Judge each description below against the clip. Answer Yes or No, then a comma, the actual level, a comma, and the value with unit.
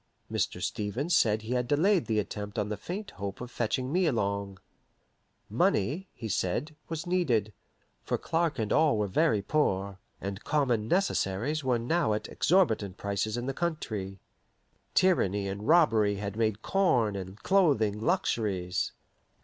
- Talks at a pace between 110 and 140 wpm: No, average, 150 wpm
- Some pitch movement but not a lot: No, wide, 7.2 semitones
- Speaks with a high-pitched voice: No, low, 110 Hz